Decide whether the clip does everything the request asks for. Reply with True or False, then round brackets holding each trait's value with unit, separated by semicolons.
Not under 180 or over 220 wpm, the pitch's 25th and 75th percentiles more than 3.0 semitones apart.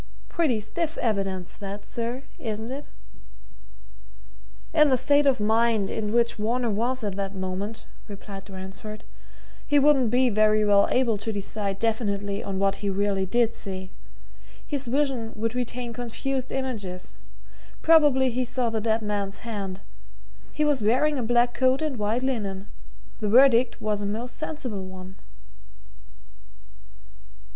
False (140 wpm; 4.0 semitones)